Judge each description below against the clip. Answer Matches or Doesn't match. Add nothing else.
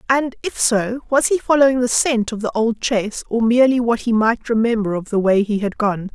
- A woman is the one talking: Matches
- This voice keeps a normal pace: Doesn't match